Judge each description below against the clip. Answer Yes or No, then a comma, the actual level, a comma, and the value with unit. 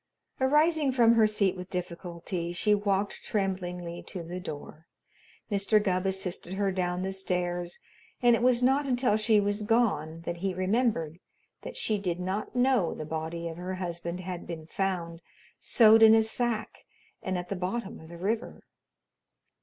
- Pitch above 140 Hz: Yes, high, 190 Hz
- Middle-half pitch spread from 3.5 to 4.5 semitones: Yes, average, 3.8 semitones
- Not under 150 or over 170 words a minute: Yes, average, 165 wpm